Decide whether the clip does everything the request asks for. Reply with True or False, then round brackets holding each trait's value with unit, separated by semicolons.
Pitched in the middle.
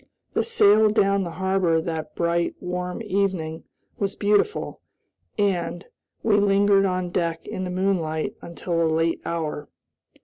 True (180 Hz)